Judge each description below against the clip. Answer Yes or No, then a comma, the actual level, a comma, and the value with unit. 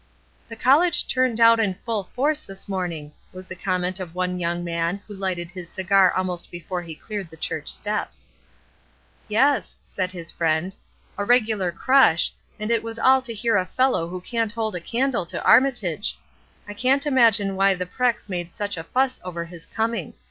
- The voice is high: Yes, high, 195 Hz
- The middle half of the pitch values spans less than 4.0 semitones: No, average, 4.5 semitones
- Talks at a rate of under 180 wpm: No, average, 185 wpm